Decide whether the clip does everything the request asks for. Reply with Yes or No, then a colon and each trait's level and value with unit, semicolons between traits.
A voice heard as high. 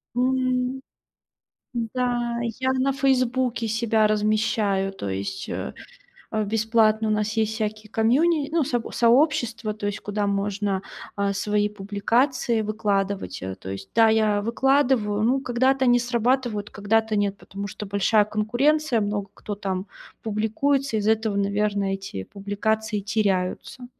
Yes: high, 215 Hz